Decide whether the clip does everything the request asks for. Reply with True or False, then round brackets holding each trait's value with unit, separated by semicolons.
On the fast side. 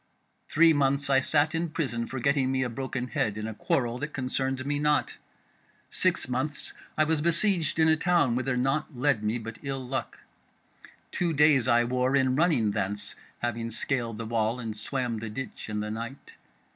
False (185 wpm)